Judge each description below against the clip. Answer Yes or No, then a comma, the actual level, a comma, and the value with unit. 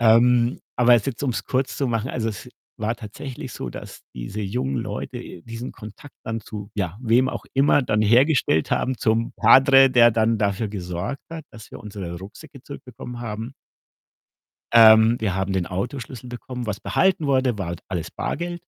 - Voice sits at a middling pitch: No, low, 115 Hz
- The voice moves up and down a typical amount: Yes, average, 3.8 semitones